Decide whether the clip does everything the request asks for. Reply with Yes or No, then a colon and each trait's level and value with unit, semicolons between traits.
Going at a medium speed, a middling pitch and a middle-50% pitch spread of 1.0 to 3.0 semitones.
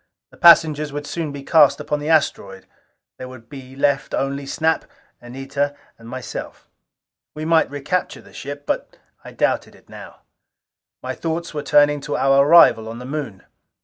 Yes: average, 165 wpm; medium, 145 Hz; narrow, 2.5 semitones